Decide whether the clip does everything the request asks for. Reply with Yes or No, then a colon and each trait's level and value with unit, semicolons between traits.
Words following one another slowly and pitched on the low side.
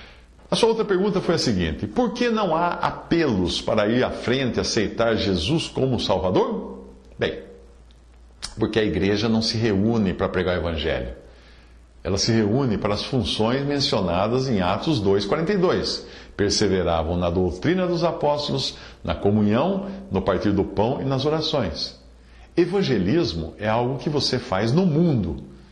No: average, 150 wpm; low, 110 Hz